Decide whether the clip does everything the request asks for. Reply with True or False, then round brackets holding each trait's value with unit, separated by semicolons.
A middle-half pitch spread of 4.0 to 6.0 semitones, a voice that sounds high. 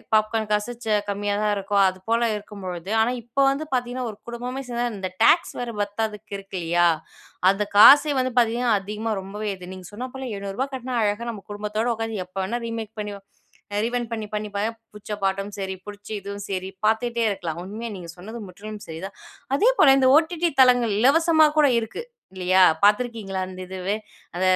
False (3.5 semitones; 215 Hz)